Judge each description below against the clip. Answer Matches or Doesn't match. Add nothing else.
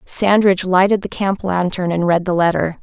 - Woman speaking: Matches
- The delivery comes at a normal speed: Matches